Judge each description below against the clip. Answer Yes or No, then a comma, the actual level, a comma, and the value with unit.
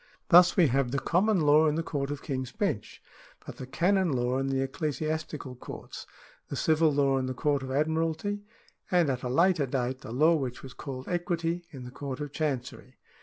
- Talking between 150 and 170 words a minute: No, average, 200 wpm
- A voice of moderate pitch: Yes, medium, 145 Hz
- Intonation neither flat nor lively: Yes, average, 3.9 semitones